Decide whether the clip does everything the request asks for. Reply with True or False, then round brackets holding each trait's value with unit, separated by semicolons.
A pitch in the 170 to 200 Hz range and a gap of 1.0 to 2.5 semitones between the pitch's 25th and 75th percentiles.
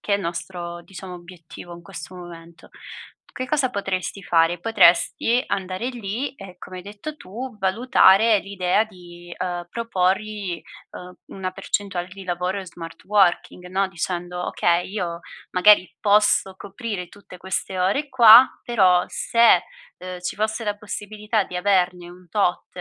False (190 Hz; 2.9 semitones)